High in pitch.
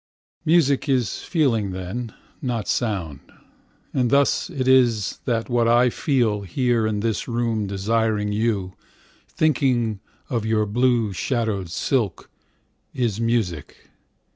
No: low, 115 Hz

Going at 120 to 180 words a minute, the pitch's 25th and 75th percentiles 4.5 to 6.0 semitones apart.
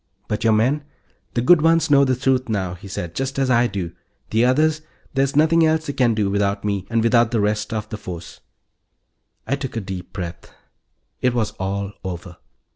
No: average, 200 wpm; average, 5.2 semitones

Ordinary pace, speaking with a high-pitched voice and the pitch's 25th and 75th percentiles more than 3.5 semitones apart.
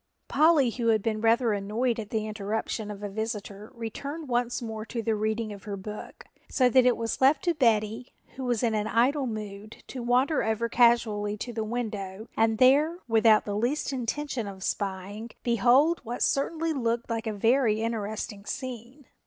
No: average, 180 wpm; high, 230 Hz; average, 2.8 semitones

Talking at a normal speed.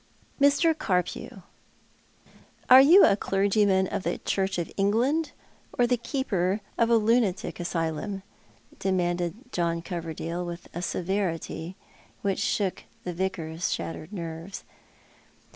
No: slow, 120 wpm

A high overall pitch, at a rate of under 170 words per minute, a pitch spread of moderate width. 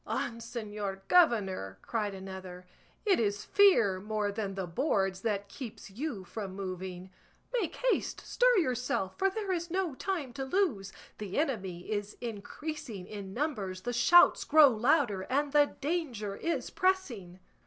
No: high, 225 Hz; average, 145 wpm; wide, 7.8 semitones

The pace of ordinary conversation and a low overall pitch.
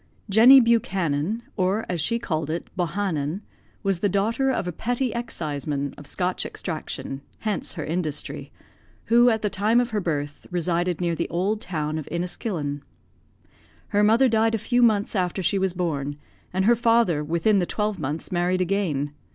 No: average, 165 wpm; medium, 185 Hz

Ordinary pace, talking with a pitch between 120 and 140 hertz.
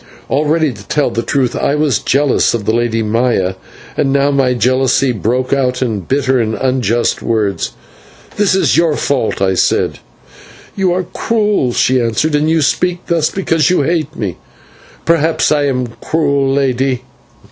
Yes: average, 160 wpm; low, 135 Hz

